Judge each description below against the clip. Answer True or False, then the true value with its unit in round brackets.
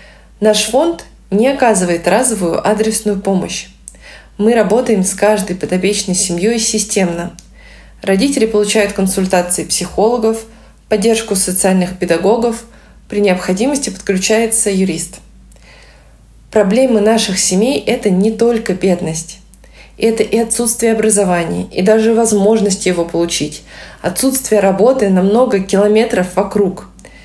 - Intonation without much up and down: False (3.2 semitones)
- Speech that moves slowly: True (105 wpm)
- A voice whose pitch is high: True (205 Hz)